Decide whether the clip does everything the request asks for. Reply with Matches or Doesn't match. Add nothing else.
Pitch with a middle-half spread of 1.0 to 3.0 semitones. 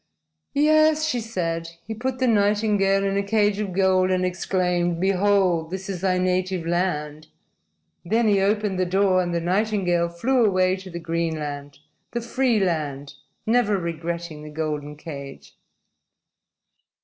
Doesn't match